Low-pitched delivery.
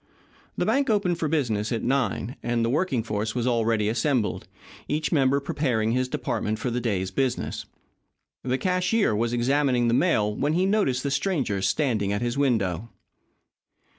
Yes: low, 125 Hz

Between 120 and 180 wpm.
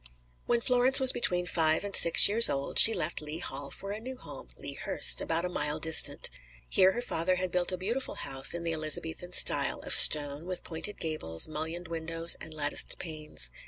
No: average, 195 wpm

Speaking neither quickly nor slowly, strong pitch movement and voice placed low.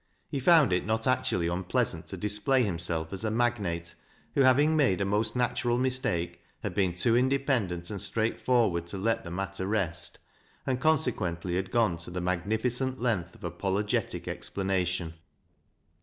Yes: average, 160 wpm; wide, 5.7 semitones; low, 100 Hz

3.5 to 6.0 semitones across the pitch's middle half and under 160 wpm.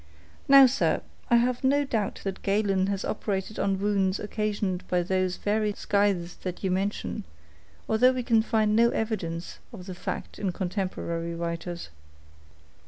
No: average, 3.0 semitones; average, 150 wpm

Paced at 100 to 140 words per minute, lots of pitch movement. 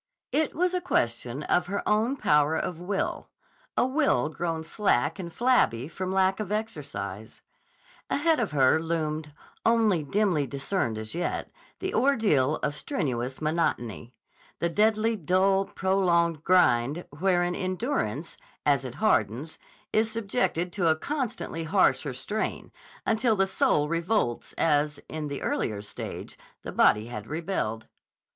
Yes: slow, 135 wpm; wide, 6.5 semitones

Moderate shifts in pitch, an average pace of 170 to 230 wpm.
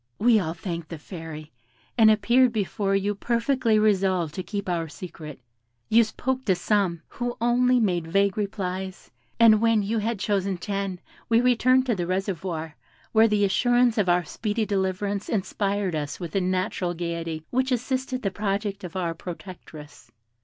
No: average, 4.0 semitones; average, 160 wpm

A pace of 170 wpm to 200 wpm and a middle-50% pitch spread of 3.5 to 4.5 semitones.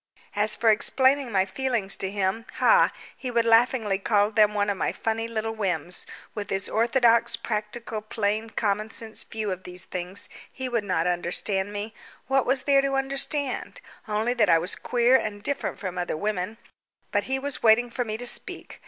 No: average, 180 wpm; average, 3.1 semitones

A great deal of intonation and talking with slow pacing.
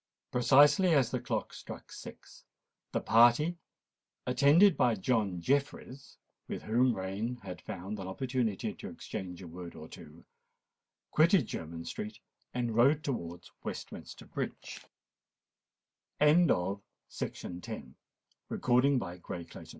Yes: wide, 6.5 semitones; slow, 100 wpm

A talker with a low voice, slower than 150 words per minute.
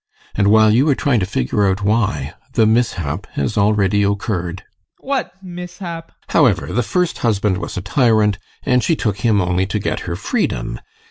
No: low, 105 Hz; average, 185 wpm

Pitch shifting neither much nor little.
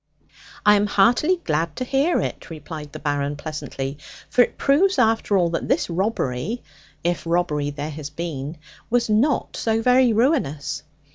No: wide, 7.9 semitones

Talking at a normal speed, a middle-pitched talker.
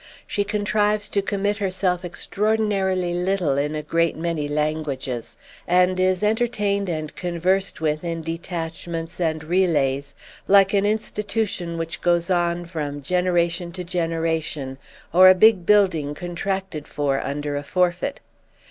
No: slow, 130 wpm; medium, 175 Hz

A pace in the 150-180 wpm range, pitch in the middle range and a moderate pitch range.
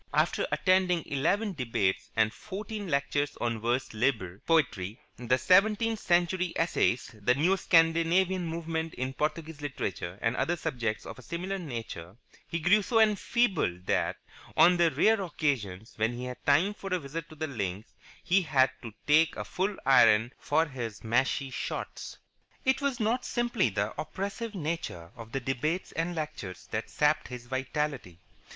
No: average, 160 wpm; medium, 150 Hz; wide, 7.1 semitones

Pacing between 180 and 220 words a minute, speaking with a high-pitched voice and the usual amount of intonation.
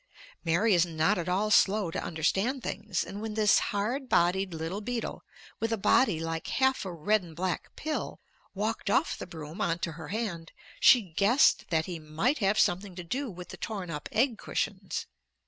Yes: average, 190 wpm; high, 195 Hz; average, 4.5 semitones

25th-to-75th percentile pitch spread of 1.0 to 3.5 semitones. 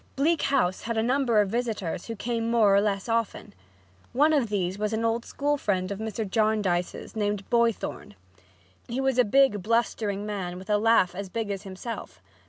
Yes: average, 2.9 semitones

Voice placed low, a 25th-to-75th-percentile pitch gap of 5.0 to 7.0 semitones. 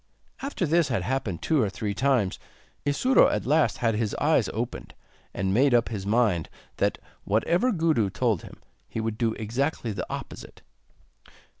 Yes: low, 115 Hz; wide, 5.4 semitones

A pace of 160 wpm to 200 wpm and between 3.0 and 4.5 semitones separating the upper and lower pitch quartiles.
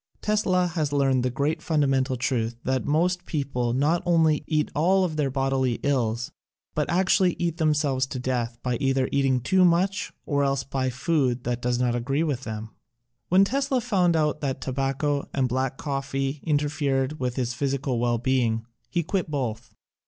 Yes: average, 175 wpm; average, 3.8 semitones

